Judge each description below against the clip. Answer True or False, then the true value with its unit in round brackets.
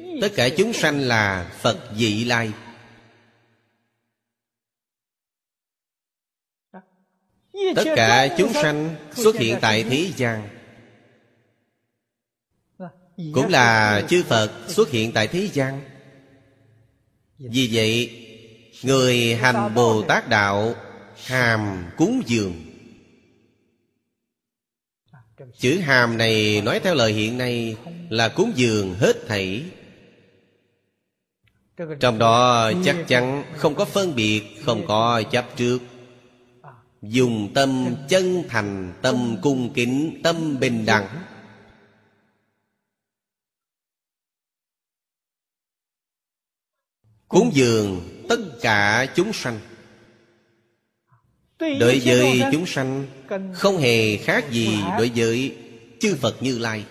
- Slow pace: True (95 wpm)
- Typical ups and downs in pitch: True (3.1 semitones)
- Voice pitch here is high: False (120 Hz)